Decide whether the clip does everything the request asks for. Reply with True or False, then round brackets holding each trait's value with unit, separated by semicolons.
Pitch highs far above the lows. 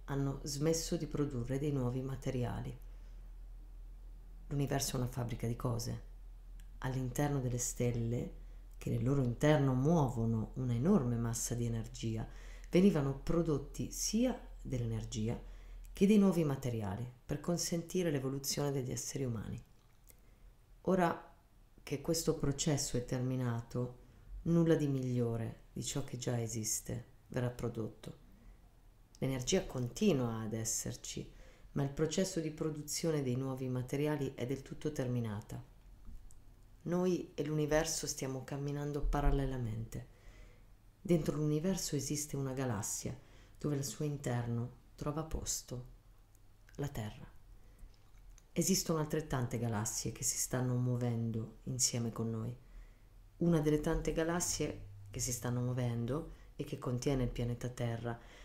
False (4.6 semitones)